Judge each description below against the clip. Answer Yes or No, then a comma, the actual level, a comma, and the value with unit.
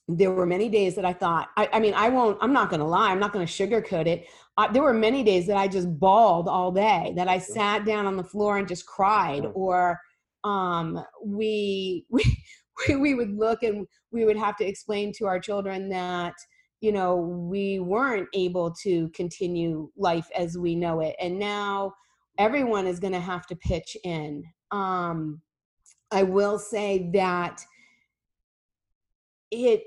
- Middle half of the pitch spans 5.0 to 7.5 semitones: No, average, 2.8 semitones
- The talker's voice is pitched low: No, high, 195 Hz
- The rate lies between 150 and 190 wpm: Yes, average, 175 wpm